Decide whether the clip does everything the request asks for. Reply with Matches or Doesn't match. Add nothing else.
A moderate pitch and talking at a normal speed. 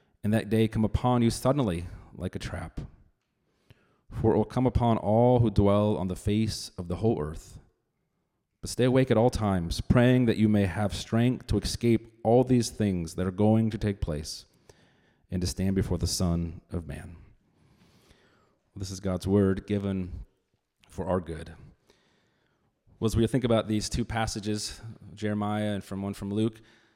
Doesn't match